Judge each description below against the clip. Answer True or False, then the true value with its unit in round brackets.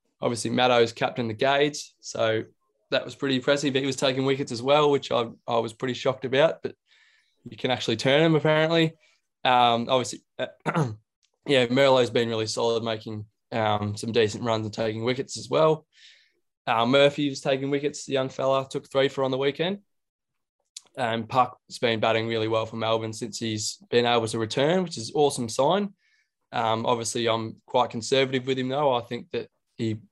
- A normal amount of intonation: True (3.9 semitones)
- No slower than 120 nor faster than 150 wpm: False (185 wpm)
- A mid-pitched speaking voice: False (125 Hz)